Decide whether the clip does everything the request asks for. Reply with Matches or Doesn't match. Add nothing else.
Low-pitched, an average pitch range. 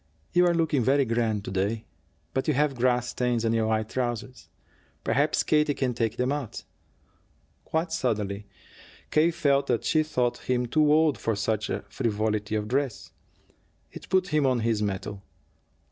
Matches